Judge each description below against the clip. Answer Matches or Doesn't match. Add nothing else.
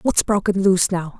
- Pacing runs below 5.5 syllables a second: Doesn't match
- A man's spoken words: Doesn't match